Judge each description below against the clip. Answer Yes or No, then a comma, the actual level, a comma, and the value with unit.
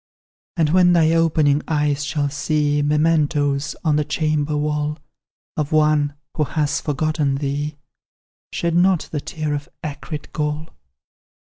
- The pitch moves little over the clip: Yes, narrow, 1.2 semitones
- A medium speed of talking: No, slow, 130 wpm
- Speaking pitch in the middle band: Yes, medium, 150 Hz